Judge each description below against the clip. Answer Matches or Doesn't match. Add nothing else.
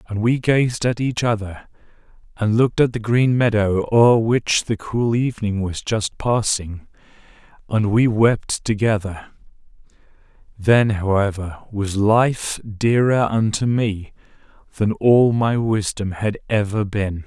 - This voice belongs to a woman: Doesn't match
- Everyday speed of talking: Doesn't match